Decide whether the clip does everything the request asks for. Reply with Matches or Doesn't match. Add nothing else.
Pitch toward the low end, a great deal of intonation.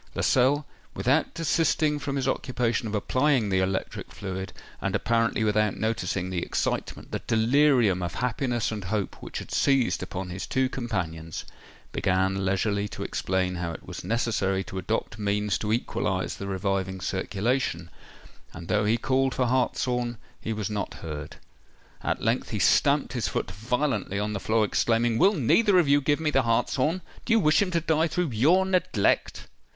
Matches